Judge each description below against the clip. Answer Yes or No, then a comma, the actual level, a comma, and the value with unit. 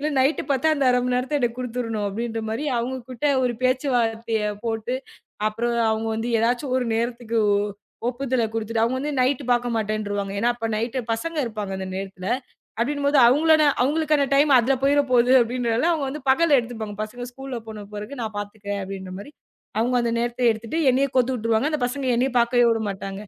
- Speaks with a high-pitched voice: Yes, high, 240 Hz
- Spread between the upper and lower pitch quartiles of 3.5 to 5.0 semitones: No, average, 3.0 semitones